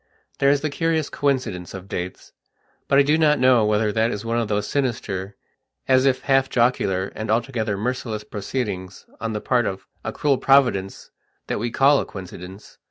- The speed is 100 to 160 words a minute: No, average, 180 wpm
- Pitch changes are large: No, average, 4.8 semitones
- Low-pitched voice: Yes, low, 115 Hz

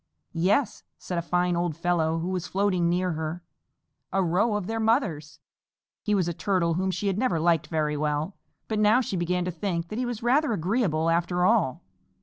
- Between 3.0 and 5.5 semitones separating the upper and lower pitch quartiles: Yes, average, 3.8 semitones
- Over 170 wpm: Yes, average, 195 wpm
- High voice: No, medium, 180 Hz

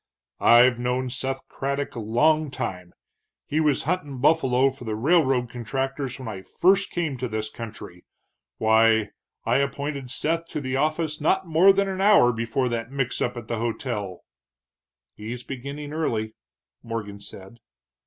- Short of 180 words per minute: Yes, average, 155 wpm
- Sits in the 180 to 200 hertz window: No, low, 130 Hz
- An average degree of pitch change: Yes, average, 4.4 semitones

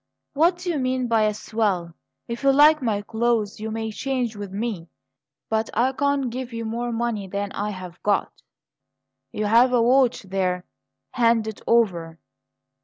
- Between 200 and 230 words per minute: No, average, 170 wpm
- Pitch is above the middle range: Yes, high, 225 Hz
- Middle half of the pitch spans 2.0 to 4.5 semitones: Yes, average, 3.6 semitones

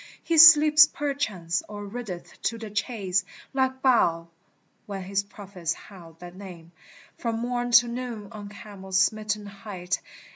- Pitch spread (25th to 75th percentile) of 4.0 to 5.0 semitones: Yes, average, 4.4 semitones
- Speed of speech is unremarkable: Yes, average, 145 wpm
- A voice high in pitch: Yes, high, 205 Hz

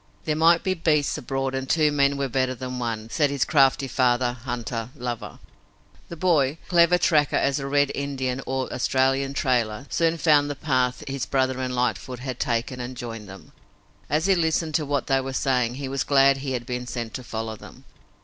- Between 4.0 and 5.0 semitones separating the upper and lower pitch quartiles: No, narrow, 2.5 semitones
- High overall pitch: No, low, 135 Hz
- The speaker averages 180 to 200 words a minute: Yes, average, 195 wpm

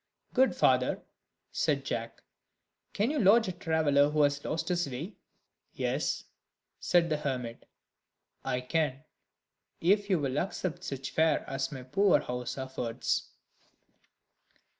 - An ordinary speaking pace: No, slow, 125 wpm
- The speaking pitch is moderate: Yes, medium, 150 Hz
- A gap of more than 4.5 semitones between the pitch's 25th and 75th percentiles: Yes, average, 5.1 semitones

